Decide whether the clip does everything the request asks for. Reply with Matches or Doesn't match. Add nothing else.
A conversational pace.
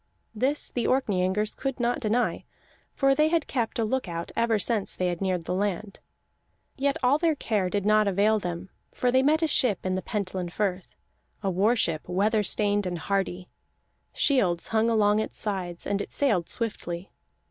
Matches